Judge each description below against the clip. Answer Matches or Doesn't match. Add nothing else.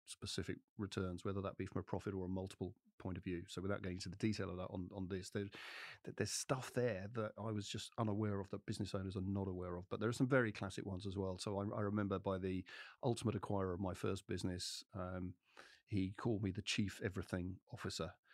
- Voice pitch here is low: Matches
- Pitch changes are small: Matches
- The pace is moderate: Doesn't match